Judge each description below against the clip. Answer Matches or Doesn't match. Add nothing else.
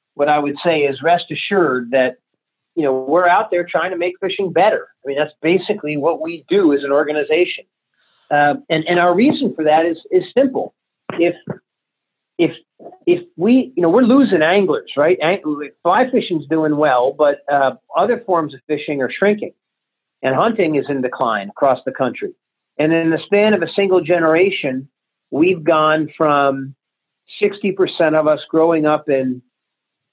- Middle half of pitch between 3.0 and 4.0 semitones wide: Doesn't match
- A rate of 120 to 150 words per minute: Doesn't match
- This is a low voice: Doesn't match